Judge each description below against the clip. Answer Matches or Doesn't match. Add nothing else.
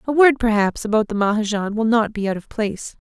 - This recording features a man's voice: Doesn't match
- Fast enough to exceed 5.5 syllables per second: Matches